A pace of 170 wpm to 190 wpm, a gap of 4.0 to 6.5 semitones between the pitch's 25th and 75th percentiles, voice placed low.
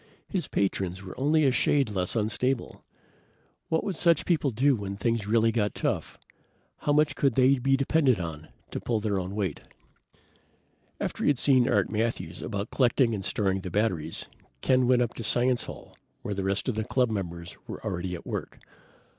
Yes: average, 185 wpm; average, 5.1 semitones; low, 115 Hz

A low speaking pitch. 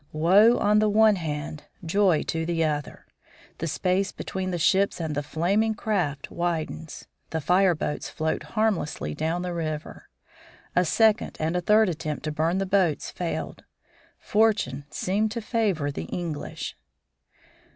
No: medium, 175 Hz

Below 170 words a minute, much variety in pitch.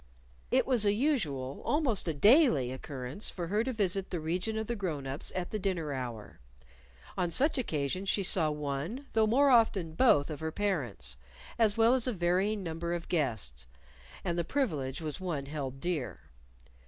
No: average, 180 wpm; wide, 7.0 semitones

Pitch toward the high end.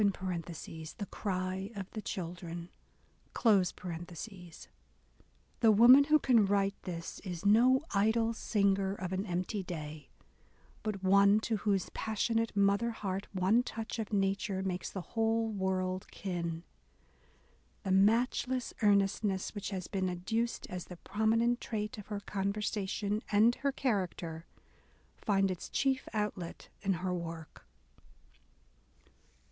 Yes: high, 195 Hz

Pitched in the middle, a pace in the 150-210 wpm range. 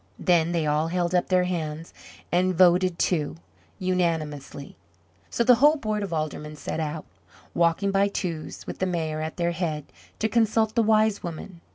Yes: medium, 175 Hz; average, 170 wpm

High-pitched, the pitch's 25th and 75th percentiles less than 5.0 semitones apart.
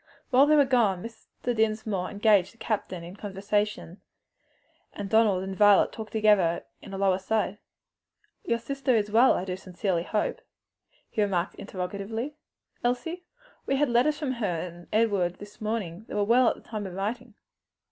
Yes: high, 210 Hz; average, 3.4 semitones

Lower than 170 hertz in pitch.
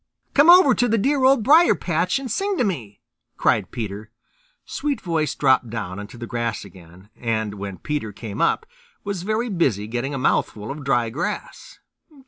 Yes: medium, 140 Hz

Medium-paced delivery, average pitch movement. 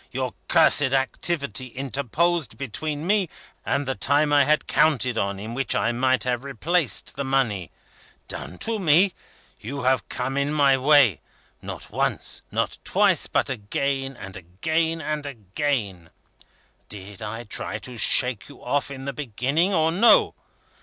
Yes: average, 150 wpm; average, 4.2 semitones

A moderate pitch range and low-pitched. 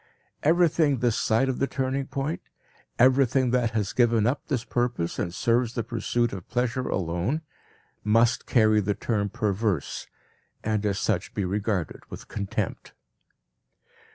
Yes: average, 3.7 semitones; low, 115 Hz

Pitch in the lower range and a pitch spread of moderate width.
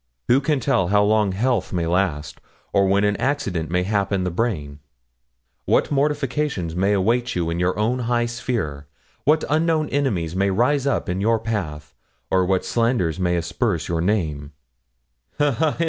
No: low, 100 Hz; wide, 5.8 semitones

